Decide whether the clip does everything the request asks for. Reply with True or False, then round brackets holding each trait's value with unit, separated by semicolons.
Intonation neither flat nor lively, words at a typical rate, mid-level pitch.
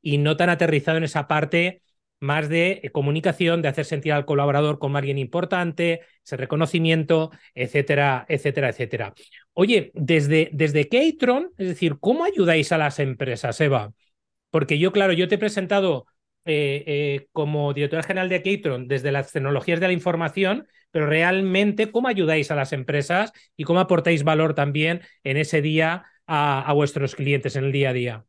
True (3.6 semitones; 170 wpm; 155 Hz)